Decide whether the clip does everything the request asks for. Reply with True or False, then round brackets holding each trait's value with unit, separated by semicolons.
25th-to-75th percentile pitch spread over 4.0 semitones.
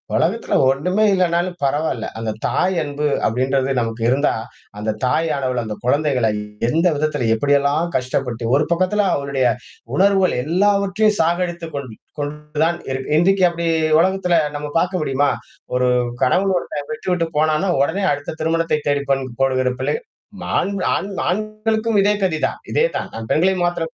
True (5.3 semitones)